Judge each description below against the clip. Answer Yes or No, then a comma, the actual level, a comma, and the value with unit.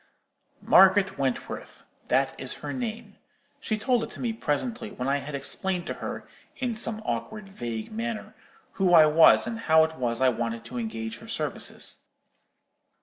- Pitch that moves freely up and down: Yes, wide, 9.0 semitones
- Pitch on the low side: No, medium, 175 Hz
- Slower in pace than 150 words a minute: No, average, 155 wpm